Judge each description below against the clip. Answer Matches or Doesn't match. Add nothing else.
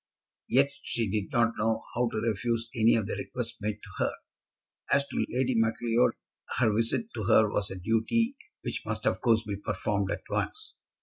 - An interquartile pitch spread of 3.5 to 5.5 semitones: Doesn't match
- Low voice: Matches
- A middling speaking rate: Matches